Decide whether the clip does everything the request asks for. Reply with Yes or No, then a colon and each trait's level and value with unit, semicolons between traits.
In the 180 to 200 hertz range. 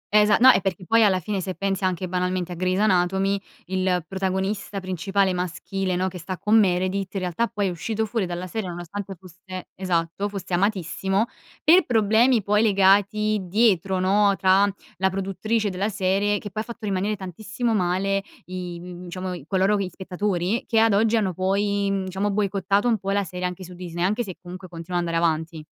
Yes: high, 190 Hz